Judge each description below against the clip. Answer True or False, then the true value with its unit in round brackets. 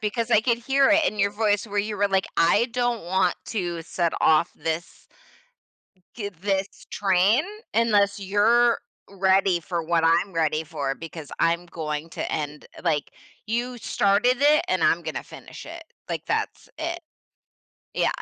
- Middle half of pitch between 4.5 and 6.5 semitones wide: True (5.5 semitones)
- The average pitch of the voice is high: True (200 Hz)